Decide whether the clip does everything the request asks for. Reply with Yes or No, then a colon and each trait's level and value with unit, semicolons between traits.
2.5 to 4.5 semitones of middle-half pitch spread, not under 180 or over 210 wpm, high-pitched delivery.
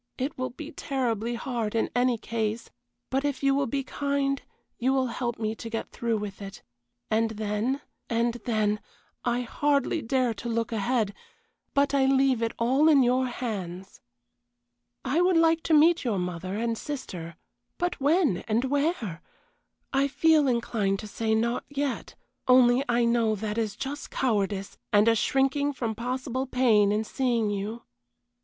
No: average, 3.7 semitones; average, 160 wpm; high, 240 Hz